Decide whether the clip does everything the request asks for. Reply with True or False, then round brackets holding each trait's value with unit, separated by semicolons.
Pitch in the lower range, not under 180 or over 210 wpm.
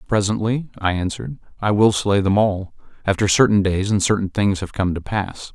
True (100 Hz; 185 wpm)